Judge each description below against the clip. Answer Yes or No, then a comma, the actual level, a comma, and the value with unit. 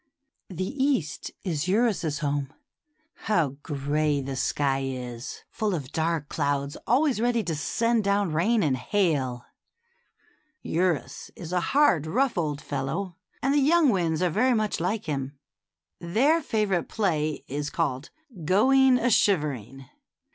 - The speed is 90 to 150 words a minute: Yes, slow, 135 wpm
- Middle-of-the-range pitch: Yes, medium, 170 Hz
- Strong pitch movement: Yes, wide, 7.1 semitones